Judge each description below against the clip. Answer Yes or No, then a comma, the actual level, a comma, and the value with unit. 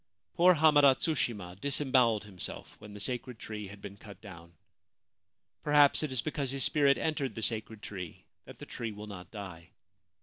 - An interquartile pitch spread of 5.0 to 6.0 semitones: Yes, wide, 5.6 semitones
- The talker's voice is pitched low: Yes, low, 115 Hz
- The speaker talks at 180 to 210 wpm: No, average, 170 wpm